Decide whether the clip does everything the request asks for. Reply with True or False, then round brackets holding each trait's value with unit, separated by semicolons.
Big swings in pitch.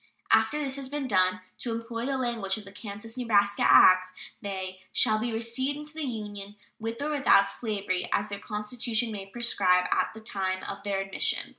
False (3.5 semitones)